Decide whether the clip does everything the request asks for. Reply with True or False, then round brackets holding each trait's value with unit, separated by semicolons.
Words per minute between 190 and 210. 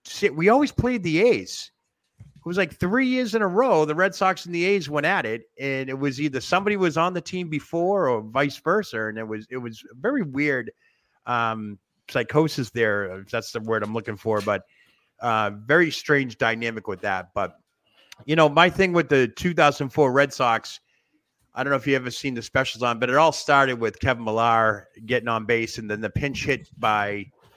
True (205 wpm)